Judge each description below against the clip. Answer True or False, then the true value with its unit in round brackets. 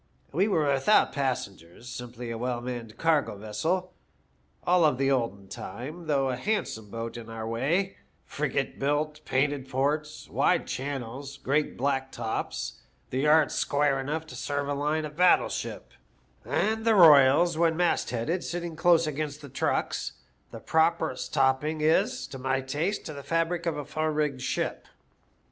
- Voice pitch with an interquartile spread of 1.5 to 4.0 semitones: True (3.7 semitones)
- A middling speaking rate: True (160 wpm)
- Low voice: False (145 Hz)